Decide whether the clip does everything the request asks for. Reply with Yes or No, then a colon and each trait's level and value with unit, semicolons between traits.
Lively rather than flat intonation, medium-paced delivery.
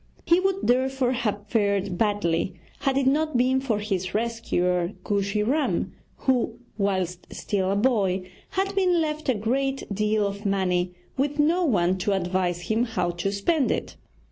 Yes: wide, 5.8 semitones; average, 160 wpm